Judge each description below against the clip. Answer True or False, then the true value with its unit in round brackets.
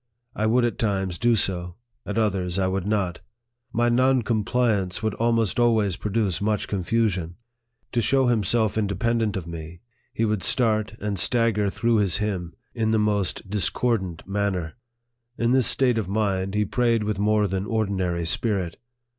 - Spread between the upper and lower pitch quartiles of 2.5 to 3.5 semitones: True (3.2 semitones)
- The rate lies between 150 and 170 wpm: True (165 wpm)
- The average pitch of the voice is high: False (105 Hz)